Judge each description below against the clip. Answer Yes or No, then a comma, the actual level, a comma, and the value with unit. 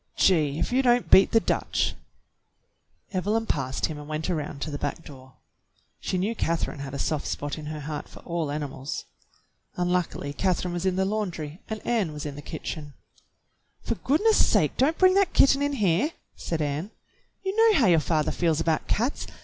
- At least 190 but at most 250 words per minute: Yes, average, 195 wpm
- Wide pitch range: Yes, wide, 6.5 semitones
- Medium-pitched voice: Yes, medium, 170 Hz